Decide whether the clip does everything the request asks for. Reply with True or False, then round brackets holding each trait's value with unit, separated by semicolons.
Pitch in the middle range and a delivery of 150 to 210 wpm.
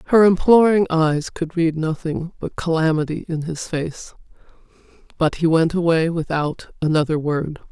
False (165 Hz; 140 wpm)